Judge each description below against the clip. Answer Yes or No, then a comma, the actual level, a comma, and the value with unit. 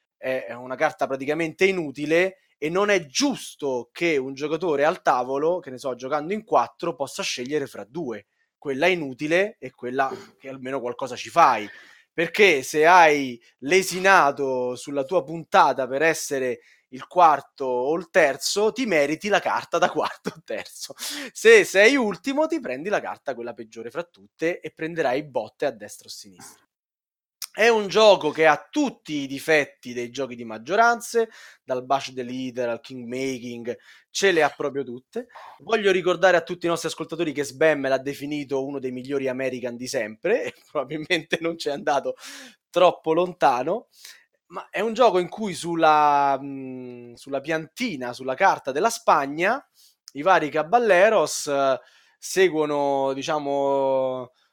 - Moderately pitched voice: Yes, medium, 150 Hz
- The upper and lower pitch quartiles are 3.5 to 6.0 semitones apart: Yes, wide, 5.6 semitones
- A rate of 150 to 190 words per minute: Yes, average, 155 wpm